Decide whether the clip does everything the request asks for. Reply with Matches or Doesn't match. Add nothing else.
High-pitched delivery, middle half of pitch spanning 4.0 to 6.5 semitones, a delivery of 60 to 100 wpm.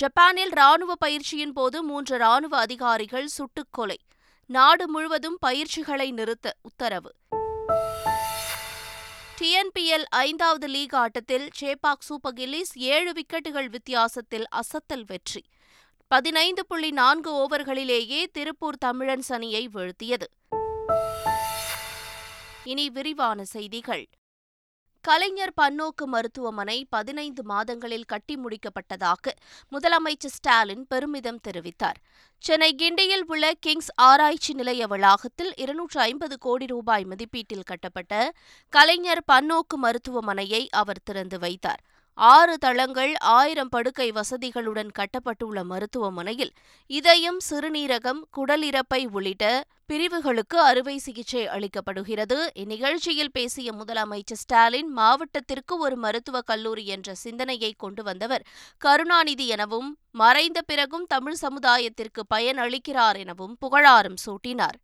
Matches